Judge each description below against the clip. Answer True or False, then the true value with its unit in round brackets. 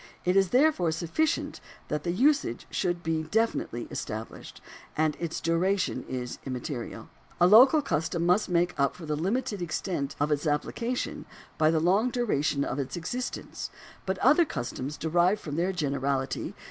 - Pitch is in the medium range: True (170 Hz)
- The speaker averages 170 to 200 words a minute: False (160 wpm)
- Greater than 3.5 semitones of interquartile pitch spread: True (5.3 semitones)